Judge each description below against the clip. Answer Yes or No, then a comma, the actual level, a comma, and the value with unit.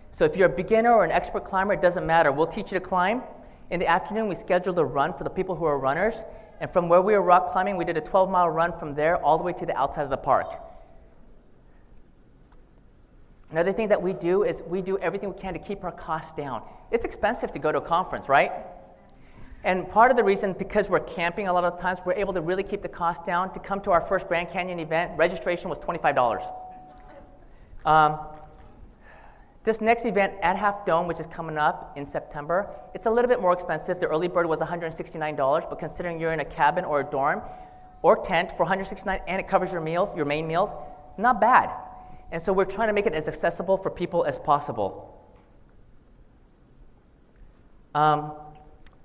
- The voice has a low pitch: No, medium, 180 Hz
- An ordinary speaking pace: No, fast, 210 wpm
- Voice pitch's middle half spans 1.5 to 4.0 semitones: Yes, average, 3.4 semitones